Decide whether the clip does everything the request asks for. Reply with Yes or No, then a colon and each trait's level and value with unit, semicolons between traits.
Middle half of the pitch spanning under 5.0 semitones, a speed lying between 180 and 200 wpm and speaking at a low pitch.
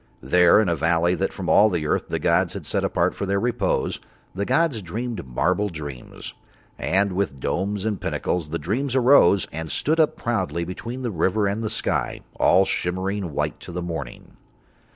Yes: average, 4.2 semitones; average, 185 wpm; very low, 95 Hz